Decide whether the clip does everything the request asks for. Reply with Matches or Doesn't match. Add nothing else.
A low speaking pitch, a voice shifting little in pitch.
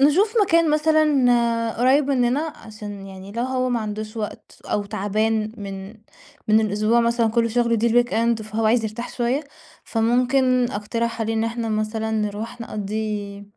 Doesn't match